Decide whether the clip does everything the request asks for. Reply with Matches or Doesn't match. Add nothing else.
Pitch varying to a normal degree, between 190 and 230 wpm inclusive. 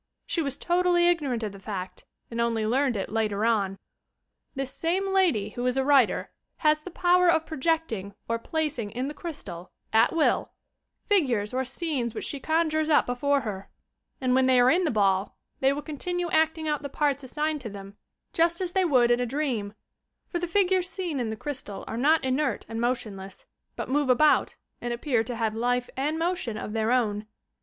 Doesn't match